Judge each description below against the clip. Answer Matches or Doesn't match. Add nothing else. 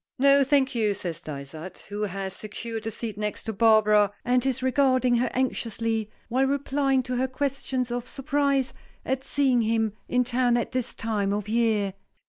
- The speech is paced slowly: Doesn't match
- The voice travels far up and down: Doesn't match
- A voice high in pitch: Matches